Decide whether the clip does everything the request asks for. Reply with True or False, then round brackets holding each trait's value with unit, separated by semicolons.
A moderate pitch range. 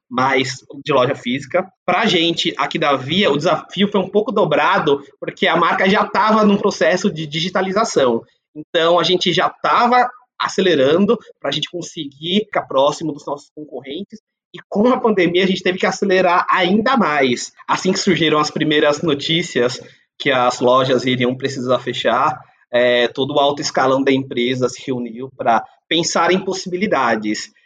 False (6.1 semitones)